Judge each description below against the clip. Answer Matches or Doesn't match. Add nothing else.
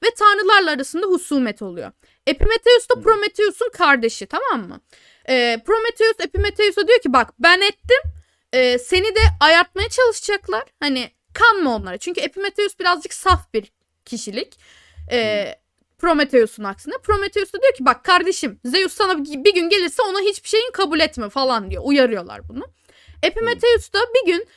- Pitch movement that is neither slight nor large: Doesn't match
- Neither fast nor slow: Doesn't match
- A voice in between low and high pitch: Doesn't match